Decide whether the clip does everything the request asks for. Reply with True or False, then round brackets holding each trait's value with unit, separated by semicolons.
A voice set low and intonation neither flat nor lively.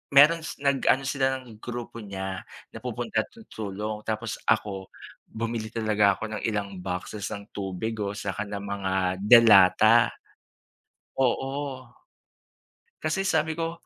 True (110 Hz; 4.2 semitones)